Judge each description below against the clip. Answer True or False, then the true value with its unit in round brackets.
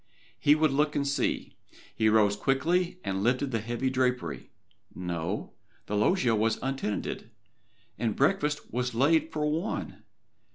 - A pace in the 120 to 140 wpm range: True (135 wpm)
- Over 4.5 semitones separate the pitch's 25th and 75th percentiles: True (5.2 semitones)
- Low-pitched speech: True (130 Hz)